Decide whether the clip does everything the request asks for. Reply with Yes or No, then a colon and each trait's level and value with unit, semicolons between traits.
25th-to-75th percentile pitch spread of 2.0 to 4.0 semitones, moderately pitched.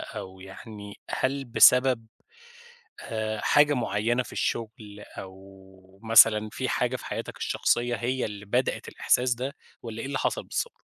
No: average, 3.6 semitones; low, 115 Hz